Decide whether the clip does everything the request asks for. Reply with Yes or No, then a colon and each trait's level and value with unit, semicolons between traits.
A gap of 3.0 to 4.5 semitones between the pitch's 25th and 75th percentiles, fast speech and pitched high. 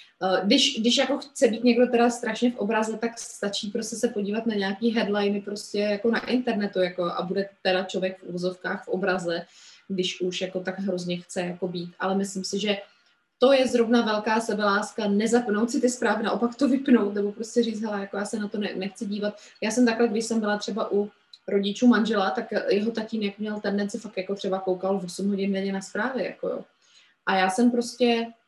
Yes: average, 3.3 semitones; fast, 205 wpm; high, 210 Hz